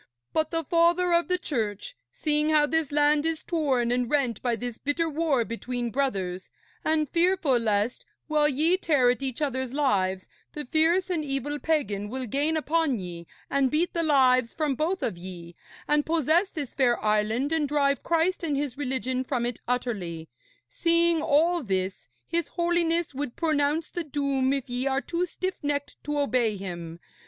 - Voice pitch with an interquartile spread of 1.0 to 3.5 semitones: No, average, 4.8 semitones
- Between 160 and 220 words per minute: Yes, average, 170 wpm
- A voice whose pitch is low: No, very high, 285 Hz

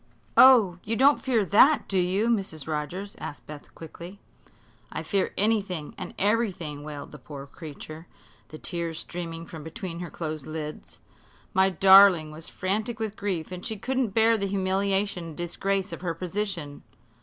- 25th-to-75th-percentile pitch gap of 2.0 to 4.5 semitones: Yes, average, 4.1 semitones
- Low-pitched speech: No, medium, 185 Hz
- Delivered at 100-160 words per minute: Yes, average, 155 wpm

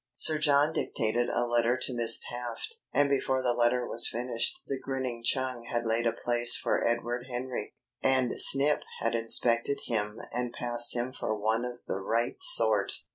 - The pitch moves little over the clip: Yes, narrow, 1.9 semitones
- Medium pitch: No, low, 120 Hz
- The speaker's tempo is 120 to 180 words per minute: Yes, average, 175 wpm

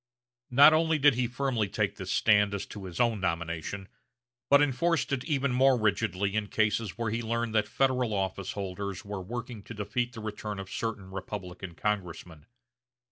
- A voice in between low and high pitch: No, low, 105 Hz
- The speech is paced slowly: No, average, 175 wpm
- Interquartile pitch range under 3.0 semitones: No, average, 4.1 semitones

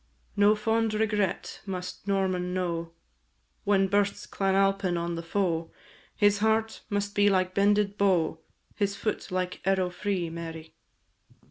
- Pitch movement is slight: Yes, narrow, 2.2 semitones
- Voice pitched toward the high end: Yes, high, 195 Hz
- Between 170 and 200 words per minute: No, slow, 135 wpm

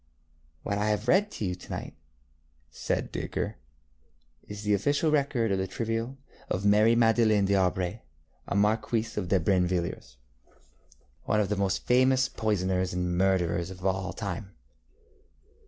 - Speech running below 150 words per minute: Yes, average, 140 wpm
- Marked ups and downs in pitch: No, average, 3.5 semitones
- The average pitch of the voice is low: Yes, low, 100 Hz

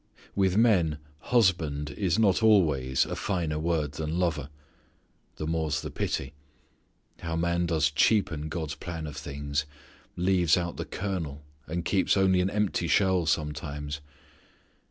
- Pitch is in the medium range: No, very low, 80 Hz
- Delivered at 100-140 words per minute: Yes, slow, 135 wpm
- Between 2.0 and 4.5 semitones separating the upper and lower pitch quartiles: Yes, average, 3.7 semitones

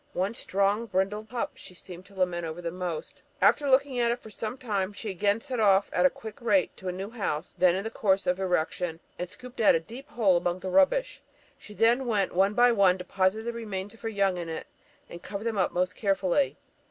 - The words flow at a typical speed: No, fast, 225 wpm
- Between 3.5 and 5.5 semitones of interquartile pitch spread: Yes, average, 3.8 semitones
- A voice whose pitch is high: Yes, high, 200 Hz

